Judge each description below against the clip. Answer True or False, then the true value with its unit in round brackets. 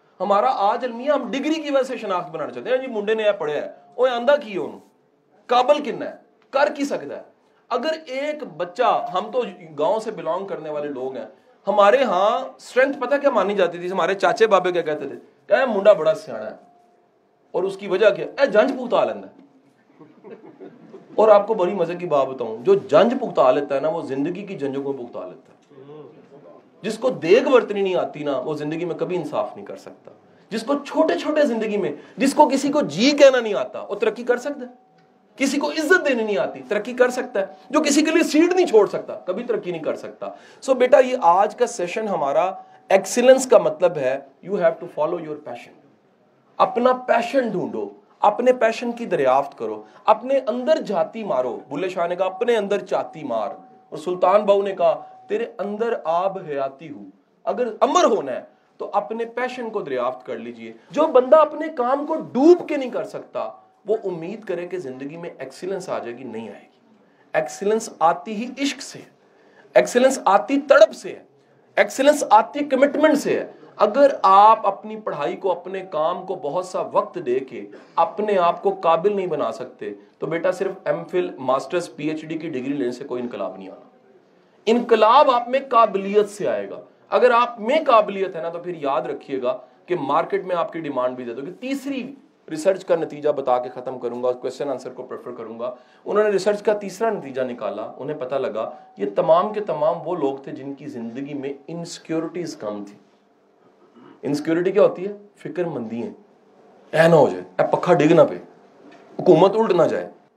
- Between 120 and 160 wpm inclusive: False (200 wpm)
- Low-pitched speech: False (205 Hz)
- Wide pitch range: True (7.5 semitones)